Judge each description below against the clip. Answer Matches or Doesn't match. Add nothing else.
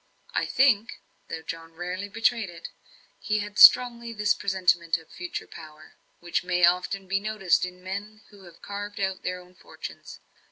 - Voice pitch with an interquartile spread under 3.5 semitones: Matches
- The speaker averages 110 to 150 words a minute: Doesn't match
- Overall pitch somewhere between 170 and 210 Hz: Matches